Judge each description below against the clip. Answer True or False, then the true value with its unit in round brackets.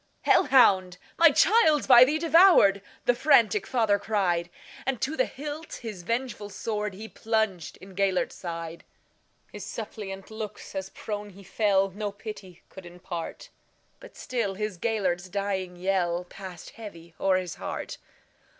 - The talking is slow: True (125 wpm)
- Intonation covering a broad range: False (3.6 semitones)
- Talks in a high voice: True (200 Hz)